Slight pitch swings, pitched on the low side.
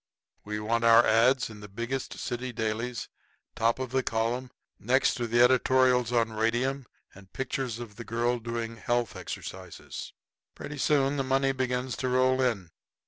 Yes: narrow, 2.2 semitones; low, 120 Hz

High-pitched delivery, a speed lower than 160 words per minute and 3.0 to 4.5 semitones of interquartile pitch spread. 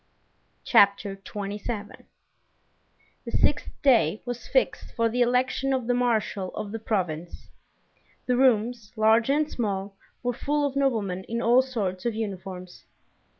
Yes: high, 225 Hz; slow, 135 wpm; average, 3.8 semitones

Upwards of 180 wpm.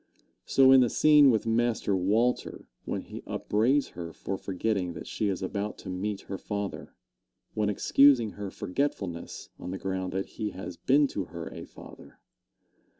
No: average, 165 wpm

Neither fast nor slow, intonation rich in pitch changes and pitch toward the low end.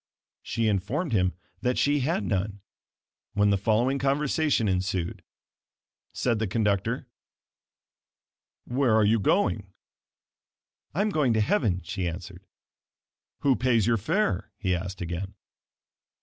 No: slow, 120 wpm; wide, 5.7 semitones; low, 110 Hz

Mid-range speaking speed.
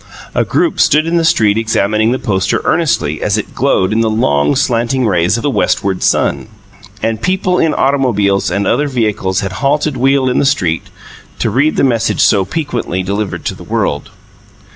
Yes: average, 185 wpm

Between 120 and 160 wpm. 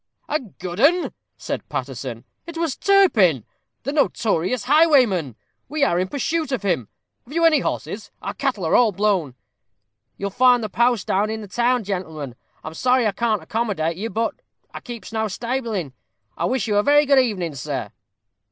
No: average, 175 wpm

